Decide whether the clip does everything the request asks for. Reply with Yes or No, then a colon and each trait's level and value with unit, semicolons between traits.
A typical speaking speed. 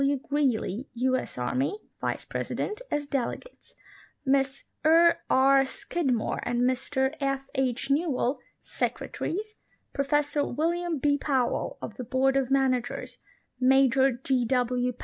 No: slow, 130 wpm